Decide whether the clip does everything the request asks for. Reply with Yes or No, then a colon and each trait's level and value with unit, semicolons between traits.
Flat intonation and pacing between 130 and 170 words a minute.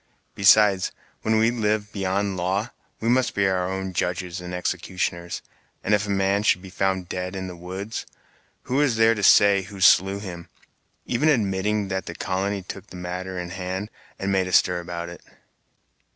No: narrow, 2.1 semitones; average, 180 wpm